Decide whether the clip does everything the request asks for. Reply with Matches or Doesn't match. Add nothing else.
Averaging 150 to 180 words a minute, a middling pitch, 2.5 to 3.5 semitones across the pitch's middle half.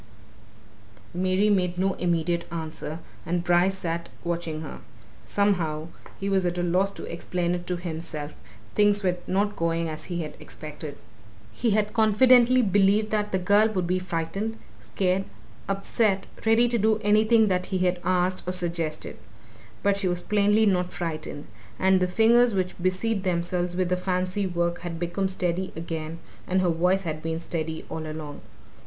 Matches